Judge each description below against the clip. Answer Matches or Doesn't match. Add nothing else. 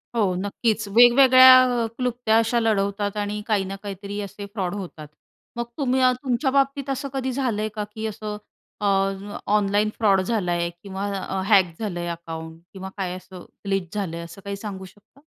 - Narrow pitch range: Doesn't match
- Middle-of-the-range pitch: Doesn't match